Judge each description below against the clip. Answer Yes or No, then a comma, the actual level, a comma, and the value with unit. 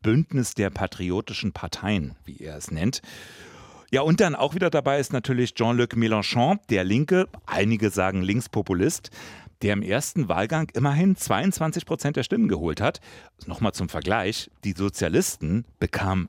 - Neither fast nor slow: Yes, average, 145 wpm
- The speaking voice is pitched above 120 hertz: No, low, 110 Hz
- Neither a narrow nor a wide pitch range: No, wide, 6.4 semitones